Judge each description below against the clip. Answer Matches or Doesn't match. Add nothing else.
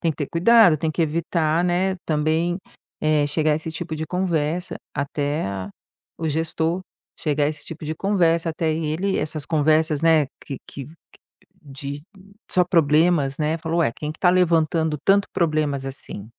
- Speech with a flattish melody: Matches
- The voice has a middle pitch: Matches